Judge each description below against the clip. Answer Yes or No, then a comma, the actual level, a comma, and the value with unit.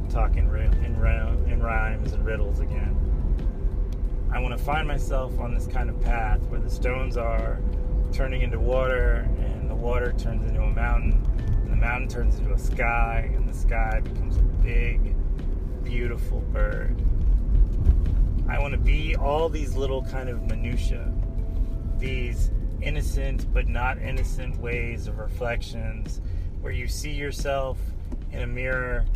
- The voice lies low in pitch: Yes, very low, 85 Hz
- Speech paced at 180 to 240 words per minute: No, average, 145 wpm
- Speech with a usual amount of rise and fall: No, wide, 6.5 semitones